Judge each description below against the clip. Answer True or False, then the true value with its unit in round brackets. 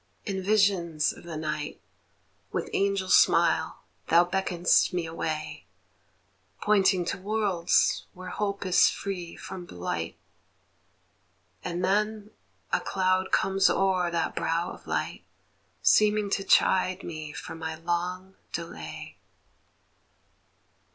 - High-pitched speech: False (180 Hz)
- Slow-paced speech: True (110 wpm)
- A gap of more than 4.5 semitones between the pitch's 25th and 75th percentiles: False (2.7 semitones)